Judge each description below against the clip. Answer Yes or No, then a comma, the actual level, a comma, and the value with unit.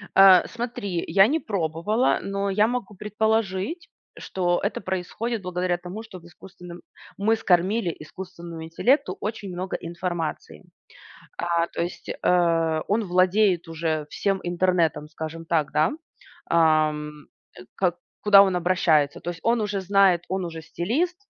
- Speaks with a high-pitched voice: No, medium, 180 Hz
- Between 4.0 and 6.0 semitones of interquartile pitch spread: No, average, 3.2 semitones